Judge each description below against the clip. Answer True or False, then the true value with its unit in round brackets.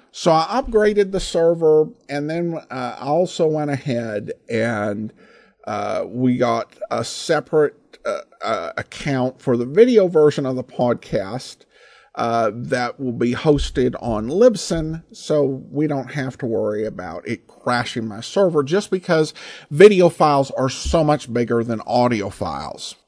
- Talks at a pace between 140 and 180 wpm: True (150 wpm)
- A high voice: False (135 Hz)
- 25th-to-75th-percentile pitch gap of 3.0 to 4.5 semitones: False (5.2 semitones)